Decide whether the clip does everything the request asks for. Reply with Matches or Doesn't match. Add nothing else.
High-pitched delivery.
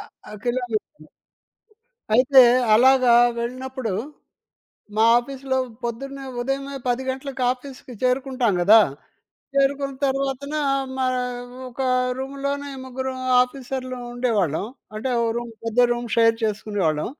Matches